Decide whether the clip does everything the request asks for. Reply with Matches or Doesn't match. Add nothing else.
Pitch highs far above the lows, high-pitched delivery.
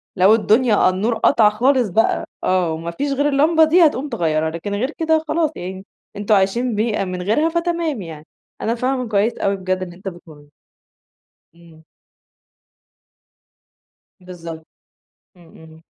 Matches